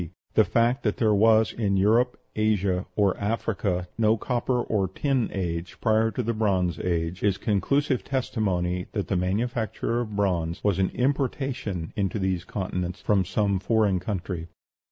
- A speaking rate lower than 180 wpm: Yes, average, 155 wpm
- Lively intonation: No, average, 3.8 semitones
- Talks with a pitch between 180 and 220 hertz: No, low, 105 Hz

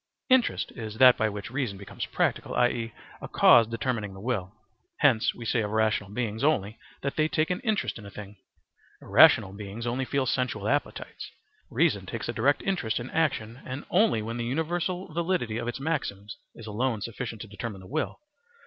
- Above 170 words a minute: Yes, average, 190 wpm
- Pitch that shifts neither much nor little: Yes, average, 4.7 semitones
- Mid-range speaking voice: No, low, 120 Hz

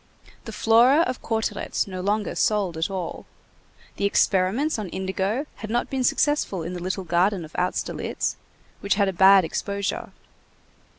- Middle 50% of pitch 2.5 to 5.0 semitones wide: Yes, average, 3.2 semitones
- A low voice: No, high, 200 Hz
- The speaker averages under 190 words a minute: Yes, average, 155 wpm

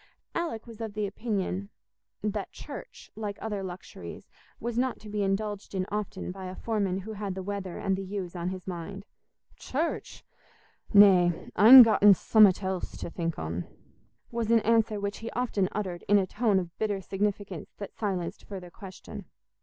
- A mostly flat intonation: Yes, narrow, 2.3 semitones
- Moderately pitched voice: No, high, 200 Hz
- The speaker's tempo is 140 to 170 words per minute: Yes, average, 165 wpm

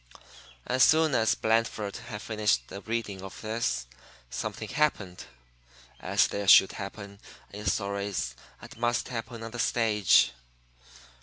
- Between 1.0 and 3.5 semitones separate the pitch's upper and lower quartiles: Yes, narrow, 2.6 semitones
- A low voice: Yes, low, 105 Hz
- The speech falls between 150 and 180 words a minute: No, slow, 135 wpm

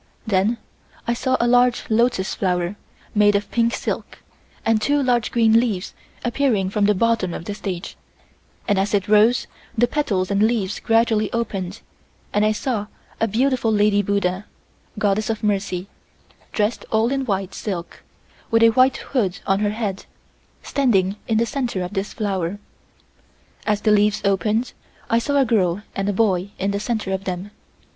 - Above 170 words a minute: No, average, 165 wpm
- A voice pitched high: Yes, high, 210 Hz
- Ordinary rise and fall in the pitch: Yes, average, 3.0 semitones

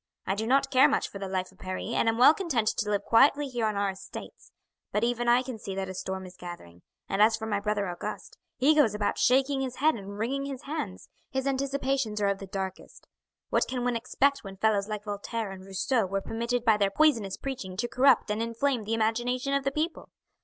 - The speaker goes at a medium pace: No, fast, 230 wpm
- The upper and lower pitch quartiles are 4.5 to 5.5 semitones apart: Yes, average, 5.0 semitones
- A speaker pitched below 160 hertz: No, high, 225 Hz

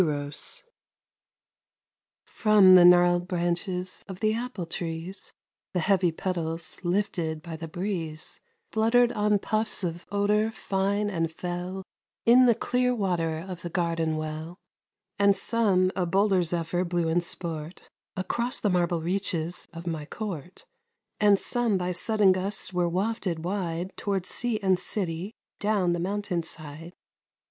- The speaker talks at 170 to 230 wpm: No, slow, 135 wpm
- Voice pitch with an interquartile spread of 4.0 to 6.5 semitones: No, average, 3.2 semitones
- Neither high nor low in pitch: Yes, medium, 180 Hz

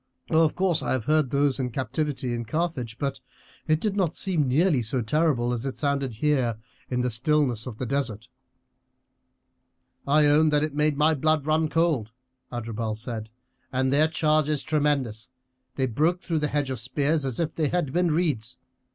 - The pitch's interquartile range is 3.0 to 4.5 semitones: Yes, average, 3.9 semitones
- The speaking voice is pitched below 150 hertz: Yes, medium, 140 Hz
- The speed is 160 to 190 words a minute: Yes, average, 180 wpm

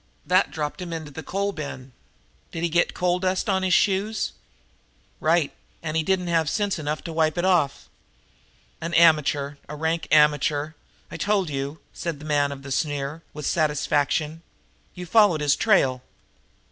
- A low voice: No, medium, 160 Hz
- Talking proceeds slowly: No, average, 165 wpm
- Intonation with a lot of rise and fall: No, average, 3.4 semitones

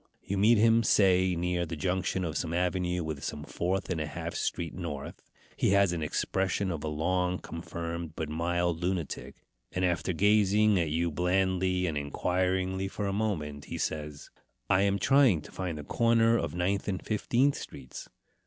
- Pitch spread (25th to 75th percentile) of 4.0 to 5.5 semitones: No, average, 2.7 semitones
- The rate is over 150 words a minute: Yes, average, 175 wpm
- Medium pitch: No, very low, 90 Hz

